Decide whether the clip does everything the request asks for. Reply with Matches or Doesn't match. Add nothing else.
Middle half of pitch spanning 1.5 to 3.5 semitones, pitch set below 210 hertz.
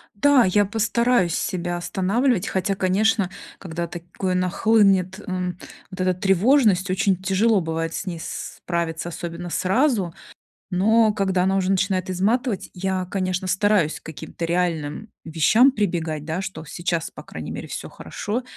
Matches